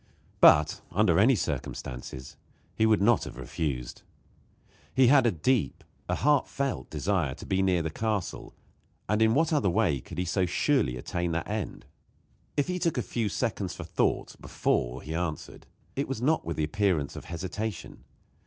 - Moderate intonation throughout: No, wide, 6.9 semitones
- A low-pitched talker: Yes, very low, 95 Hz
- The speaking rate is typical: Yes, average, 170 wpm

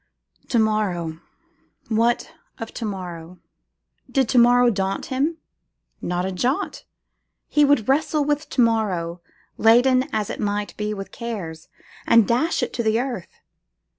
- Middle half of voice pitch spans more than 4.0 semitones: Yes, average, 4.6 semitones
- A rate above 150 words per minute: No, average, 140 wpm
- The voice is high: Yes, high, 225 Hz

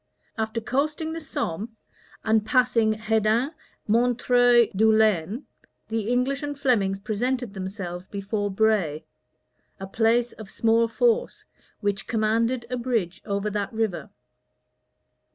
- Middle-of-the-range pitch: No, high, 220 Hz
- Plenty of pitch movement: No, average, 3.3 semitones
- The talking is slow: Yes, slow, 115 wpm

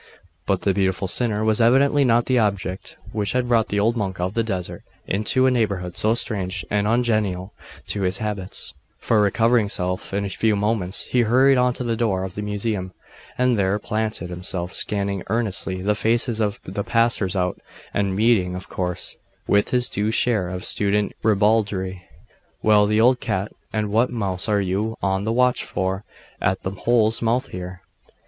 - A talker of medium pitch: No, low, 105 Hz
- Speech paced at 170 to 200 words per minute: Yes, average, 180 wpm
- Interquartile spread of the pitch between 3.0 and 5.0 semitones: Yes, average, 3.3 semitones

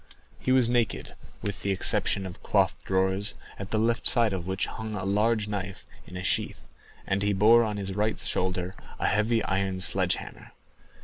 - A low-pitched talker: Yes, low, 100 Hz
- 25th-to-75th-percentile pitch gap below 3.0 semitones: Yes, narrow, 2.5 semitones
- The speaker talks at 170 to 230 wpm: Yes, average, 185 wpm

